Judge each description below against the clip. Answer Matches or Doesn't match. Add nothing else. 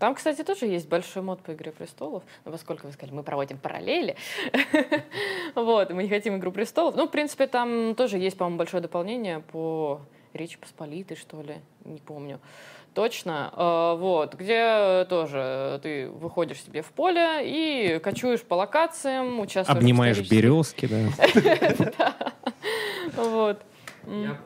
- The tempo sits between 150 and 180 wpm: Doesn't match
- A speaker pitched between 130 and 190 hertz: Matches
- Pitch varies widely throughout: Matches